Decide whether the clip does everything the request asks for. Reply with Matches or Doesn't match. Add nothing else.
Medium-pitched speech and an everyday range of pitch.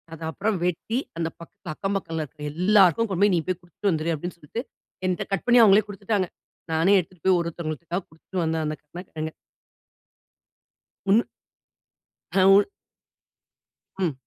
Matches